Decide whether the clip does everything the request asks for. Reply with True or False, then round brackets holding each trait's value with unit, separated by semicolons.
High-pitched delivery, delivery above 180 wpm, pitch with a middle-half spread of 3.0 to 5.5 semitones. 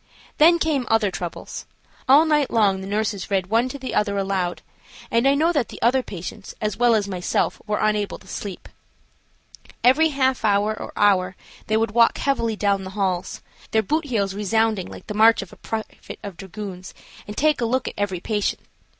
True (215 Hz; 195 wpm; 3.8 semitones)